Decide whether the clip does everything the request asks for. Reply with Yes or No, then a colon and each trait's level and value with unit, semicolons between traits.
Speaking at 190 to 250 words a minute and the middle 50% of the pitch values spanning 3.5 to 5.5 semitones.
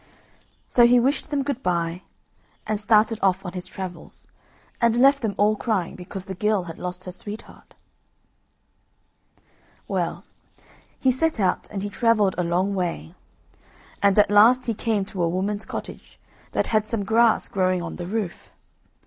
No: average, 160 wpm; average, 3.8 semitones